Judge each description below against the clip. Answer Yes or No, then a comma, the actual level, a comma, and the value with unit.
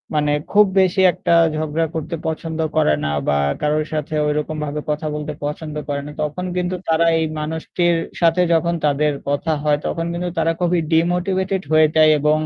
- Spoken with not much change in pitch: Yes, narrow, 2.2 semitones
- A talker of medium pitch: Yes, medium, 160 Hz